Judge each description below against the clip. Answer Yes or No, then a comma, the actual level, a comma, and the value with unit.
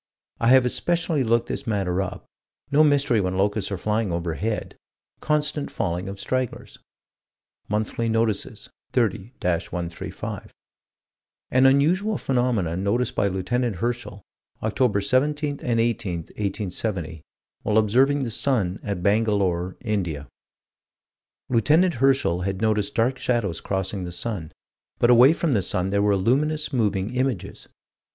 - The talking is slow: Yes, slow, 130 wpm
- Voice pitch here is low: Yes, low, 110 Hz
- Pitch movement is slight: No, average, 5.0 semitones